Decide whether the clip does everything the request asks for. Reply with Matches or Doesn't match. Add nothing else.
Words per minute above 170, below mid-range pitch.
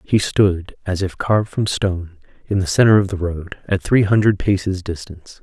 Matches